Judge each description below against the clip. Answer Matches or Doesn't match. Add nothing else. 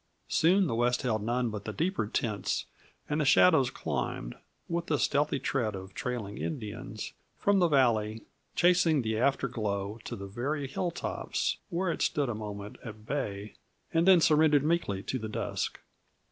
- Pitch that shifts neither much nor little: Doesn't match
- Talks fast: Doesn't match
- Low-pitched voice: Matches